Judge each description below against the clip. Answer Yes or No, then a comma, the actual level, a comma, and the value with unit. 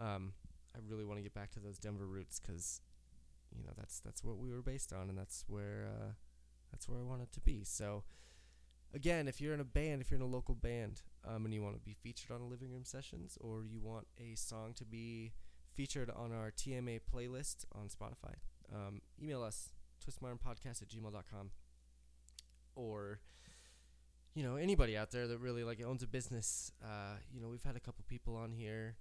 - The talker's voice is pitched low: Yes, low, 110 Hz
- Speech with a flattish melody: No, average, 4.2 semitones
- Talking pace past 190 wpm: Yes, average, 200 wpm